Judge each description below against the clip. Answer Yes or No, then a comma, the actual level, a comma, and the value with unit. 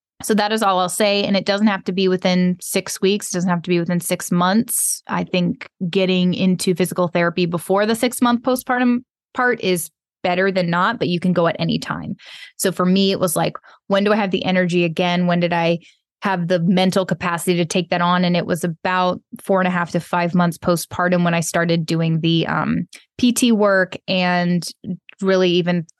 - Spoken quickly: Yes, fast, 215 wpm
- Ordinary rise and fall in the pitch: No, narrow, 1.9 semitones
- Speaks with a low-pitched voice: No, medium, 185 Hz